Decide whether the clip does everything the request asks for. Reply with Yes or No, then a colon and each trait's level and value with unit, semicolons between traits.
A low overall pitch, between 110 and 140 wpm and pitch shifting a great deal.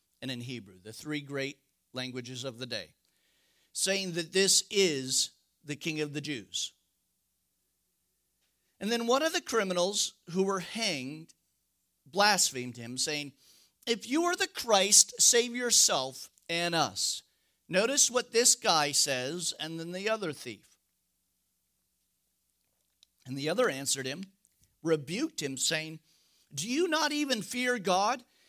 No: medium, 165 Hz; slow, 135 wpm; wide, 8.5 semitones